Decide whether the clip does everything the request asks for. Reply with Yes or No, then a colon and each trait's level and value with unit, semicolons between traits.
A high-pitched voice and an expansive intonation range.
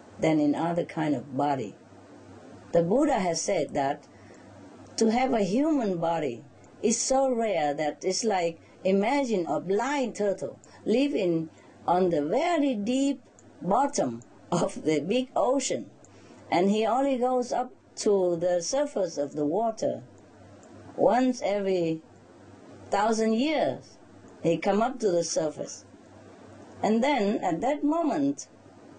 Yes: high, 220 Hz; wide, 7.4 semitones